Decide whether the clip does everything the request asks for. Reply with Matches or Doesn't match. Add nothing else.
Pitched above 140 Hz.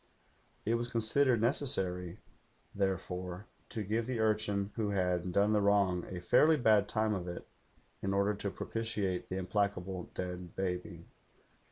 Doesn't match